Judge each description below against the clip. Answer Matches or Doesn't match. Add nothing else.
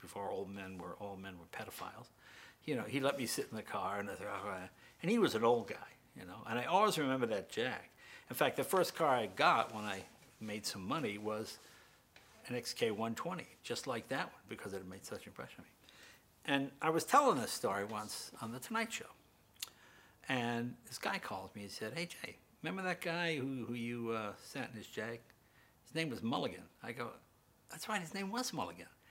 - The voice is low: Matches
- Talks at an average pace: Doesn't match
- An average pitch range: Doesn't match